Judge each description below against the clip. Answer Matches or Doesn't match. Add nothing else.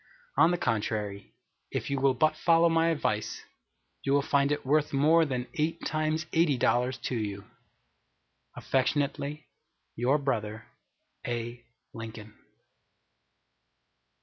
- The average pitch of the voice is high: Doesn't match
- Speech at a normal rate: Doesn't match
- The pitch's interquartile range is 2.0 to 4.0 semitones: Doesn't match